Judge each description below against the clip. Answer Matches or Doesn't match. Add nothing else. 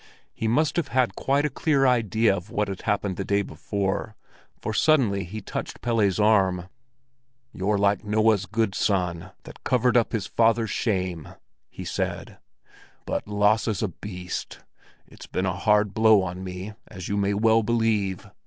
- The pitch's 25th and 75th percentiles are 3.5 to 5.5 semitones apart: Doesn't match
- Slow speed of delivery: Doesn't match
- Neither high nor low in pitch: Doesn't match